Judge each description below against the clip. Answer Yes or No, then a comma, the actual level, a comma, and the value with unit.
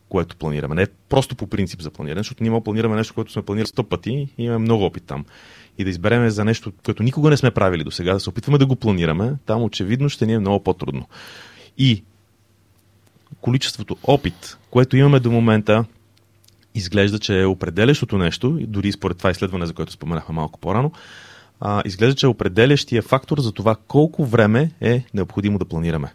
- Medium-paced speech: No, fast, 190 wpm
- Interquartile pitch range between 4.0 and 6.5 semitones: No, average, 3.5 semitones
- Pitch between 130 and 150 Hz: No, low, 110 Hz